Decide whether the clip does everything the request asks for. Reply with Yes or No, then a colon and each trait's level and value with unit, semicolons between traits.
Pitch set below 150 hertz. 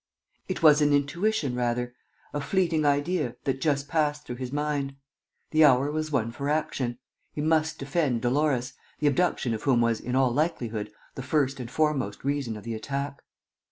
Yes: medium, 140 Hz